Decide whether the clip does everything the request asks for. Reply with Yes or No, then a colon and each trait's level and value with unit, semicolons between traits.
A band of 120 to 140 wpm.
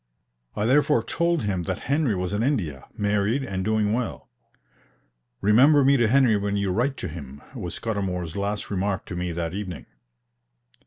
No: average, 165 wpm